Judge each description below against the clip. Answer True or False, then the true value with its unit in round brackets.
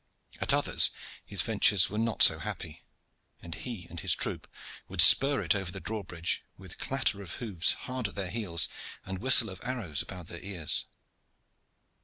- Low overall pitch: True (95 Hz)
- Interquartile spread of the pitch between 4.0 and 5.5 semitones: True (4.6 semitones)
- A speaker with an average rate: True (170 wpm)